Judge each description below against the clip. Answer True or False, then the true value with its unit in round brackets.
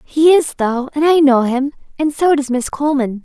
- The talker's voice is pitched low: False (280 Hz)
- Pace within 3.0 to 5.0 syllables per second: True (4.9 syllables/s)